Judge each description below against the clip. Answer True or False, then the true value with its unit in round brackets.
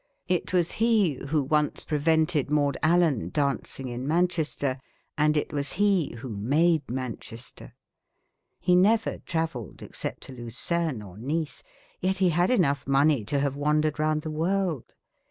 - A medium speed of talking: True (145 wpm)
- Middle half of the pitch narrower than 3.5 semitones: False (3.9 semitones)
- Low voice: False (150 Hz)